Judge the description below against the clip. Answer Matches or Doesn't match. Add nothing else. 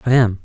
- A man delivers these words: Matches